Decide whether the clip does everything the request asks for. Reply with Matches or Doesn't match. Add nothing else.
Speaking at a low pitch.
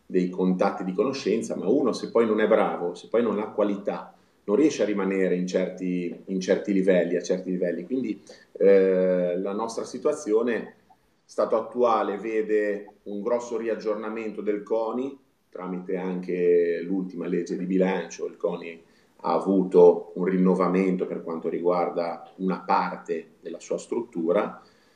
Matches